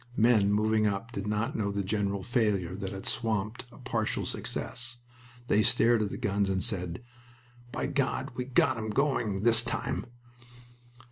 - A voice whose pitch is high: No, low, 110 Hz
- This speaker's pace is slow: No, average, 160 wpm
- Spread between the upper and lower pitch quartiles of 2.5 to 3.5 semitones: Yes, average, 3.0 semitones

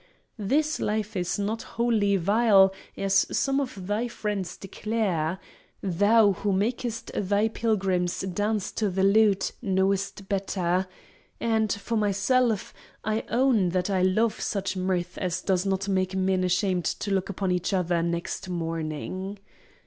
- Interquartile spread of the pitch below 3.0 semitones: Yes, narrow, 2.6 semitones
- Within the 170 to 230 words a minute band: No, average, 140 wpm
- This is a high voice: Yes, high, 195 Hz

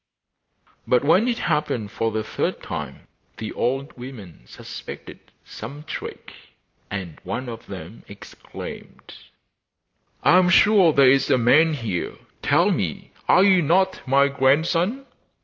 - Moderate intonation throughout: No, wide, 6.7 semitones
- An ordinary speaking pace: No, slow, 130 wpm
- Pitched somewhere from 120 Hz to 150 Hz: Yes, low, 135 Hz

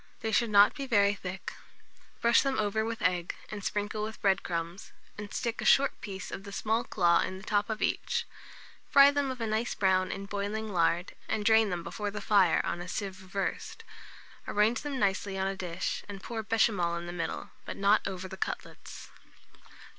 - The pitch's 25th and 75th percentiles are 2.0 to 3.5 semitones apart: Yes, average, 2.7 semitones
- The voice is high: Yes, high, 205 Hz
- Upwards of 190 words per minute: Yes, average, 200 wpm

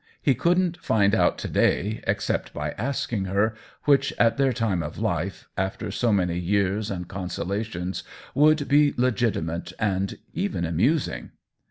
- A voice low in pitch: Yes, low, 105 Hz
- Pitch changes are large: Yes, wide, 6.3 semitones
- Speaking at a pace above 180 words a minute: No, average, 145 wpm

